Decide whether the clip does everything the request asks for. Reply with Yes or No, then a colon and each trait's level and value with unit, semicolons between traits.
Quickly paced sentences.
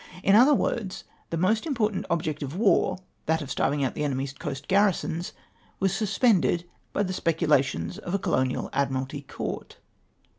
No: average, 175 wpm